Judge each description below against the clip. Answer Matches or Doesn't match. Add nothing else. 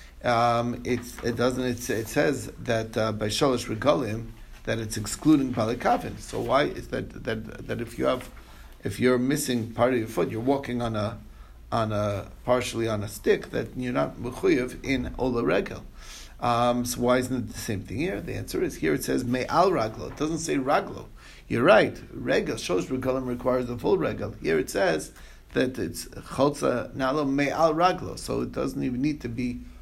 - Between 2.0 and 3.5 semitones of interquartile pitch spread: Matches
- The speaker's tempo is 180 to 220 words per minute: Matches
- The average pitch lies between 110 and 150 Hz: Matches